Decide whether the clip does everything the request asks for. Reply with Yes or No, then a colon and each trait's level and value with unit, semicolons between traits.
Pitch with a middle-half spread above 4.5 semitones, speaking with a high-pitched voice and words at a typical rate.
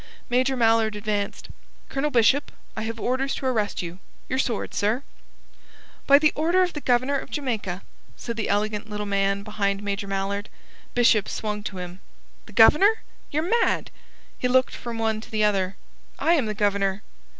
No: average, 4.2 semitones; high, 220 Hz; average, 165 wpm